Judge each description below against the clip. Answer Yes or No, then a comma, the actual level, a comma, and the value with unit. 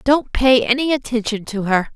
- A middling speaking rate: Yes, average, 185 wpm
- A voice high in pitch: Yes, high, 240 Hz